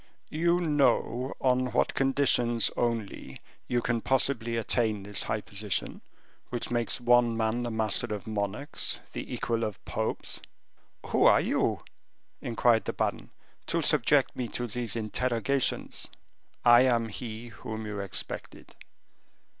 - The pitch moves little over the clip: Yes, narrow, 2.1 semitones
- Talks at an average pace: No, slow, 130 wpm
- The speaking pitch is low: Yes, low, 120 Hz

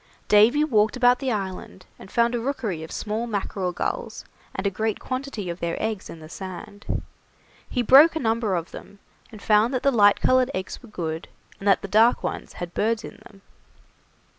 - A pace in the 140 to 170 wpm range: No, average, 195 wpm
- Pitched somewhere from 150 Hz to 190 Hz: No, high, 215 Hz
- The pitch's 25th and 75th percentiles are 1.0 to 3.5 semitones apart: No, average, 4.3 semitones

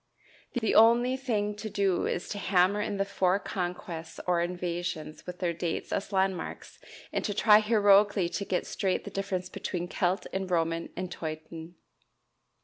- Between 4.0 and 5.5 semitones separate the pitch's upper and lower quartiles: No, narrow, 2.6 semitones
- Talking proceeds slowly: No, average, 160 wpm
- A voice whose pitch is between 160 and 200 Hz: Yes, medium, 185 Hz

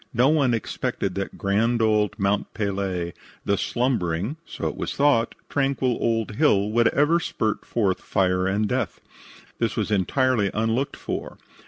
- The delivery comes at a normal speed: Yes, average, 150 wpm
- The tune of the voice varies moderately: Yes, average, 4.4 semitones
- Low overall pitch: Yes, low, 110 Hz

